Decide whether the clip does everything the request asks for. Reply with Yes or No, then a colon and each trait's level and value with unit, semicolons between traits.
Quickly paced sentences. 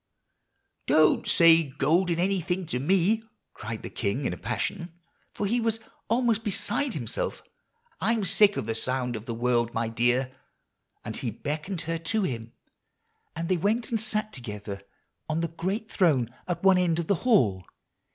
No: average, 165 wpm